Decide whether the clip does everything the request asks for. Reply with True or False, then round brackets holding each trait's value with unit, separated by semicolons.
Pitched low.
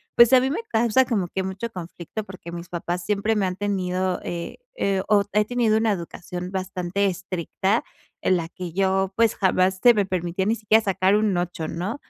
False (190 Hz)